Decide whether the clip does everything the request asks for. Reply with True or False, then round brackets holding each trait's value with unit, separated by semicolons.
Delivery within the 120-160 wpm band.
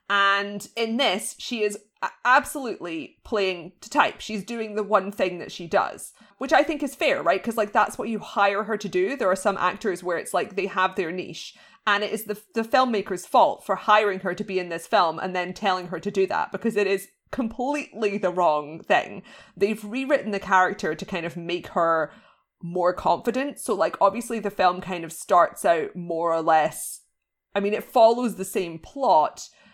False (205 wpm)